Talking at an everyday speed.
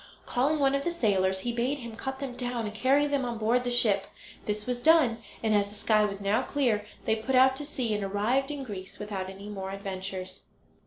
No: fast, 225 wpm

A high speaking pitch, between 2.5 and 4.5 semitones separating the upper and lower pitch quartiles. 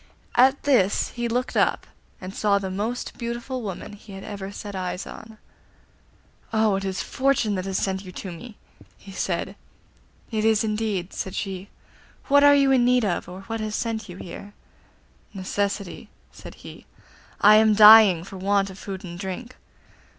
Yes: high, 205 Hz; average, 2.9 semitones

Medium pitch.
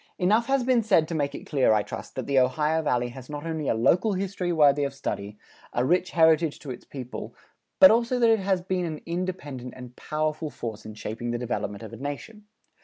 Yes: medium, 155 Hz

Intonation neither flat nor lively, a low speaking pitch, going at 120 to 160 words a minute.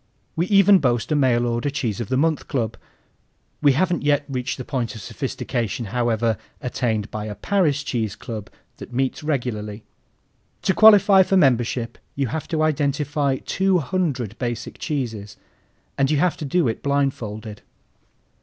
Yes: average, 4.7 semitones; low, 130 Hz; average, 155 wpm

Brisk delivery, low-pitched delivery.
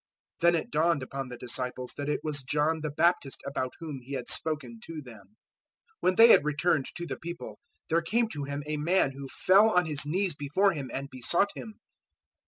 No: fast, 210 wpm; medium, 150 Hz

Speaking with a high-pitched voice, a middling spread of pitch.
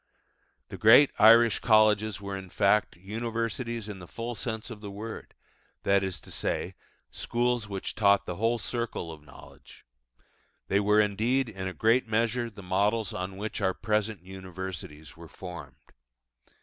No: low, 105 Hz; average, 3.2 semitones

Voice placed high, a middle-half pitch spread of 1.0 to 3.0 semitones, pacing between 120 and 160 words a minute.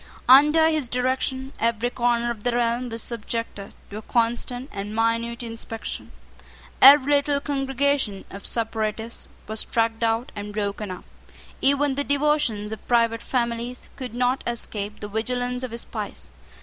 Yes: high, 235 Hz; narrow, 2.6 semitones; average, 150 wpm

